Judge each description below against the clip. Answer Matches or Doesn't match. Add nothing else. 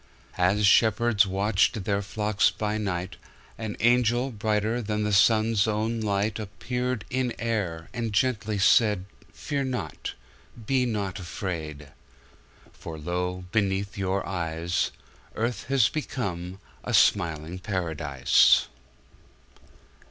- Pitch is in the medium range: Doesn't match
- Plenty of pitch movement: Doesn't match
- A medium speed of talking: Doesn't match